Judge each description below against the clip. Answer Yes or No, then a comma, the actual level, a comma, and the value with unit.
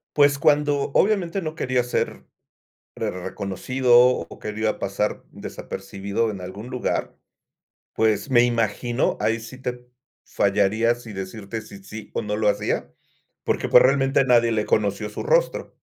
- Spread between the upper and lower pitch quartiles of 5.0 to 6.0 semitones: No, average, 3.8 semitones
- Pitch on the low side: Yes, low, 115 Hz